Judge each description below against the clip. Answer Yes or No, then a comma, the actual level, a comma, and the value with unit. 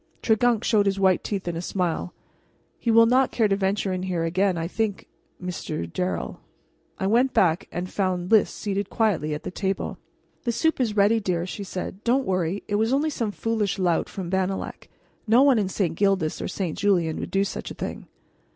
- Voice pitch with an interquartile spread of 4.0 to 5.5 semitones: No, average, 3.4 semitones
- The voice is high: Yes, high, 195 Hz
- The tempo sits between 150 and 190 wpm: No, average, 200 wpm